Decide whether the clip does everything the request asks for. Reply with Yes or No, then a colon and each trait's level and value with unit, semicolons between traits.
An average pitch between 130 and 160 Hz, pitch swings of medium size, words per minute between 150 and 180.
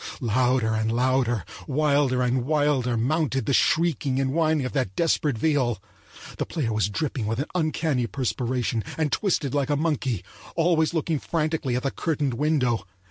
Yes: low, 135 Hz; average, 4.0 semitones; average, 160 wpm